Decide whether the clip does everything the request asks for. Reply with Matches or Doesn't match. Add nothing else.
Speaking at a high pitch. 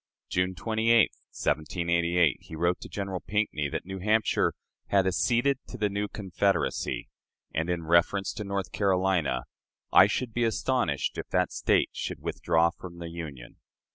Doesn't match